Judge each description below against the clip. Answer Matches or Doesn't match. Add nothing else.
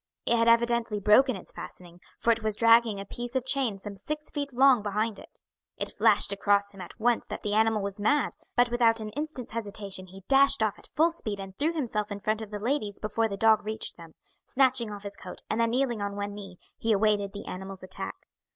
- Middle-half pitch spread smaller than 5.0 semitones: Matches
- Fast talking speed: Matches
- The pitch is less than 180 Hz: Doesn't match